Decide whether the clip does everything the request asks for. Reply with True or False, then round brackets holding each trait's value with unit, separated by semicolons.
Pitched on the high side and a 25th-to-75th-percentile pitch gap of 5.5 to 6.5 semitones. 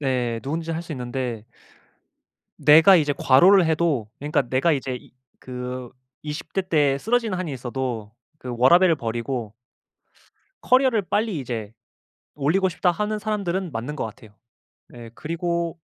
False (150 Hz; 5.9 semitones)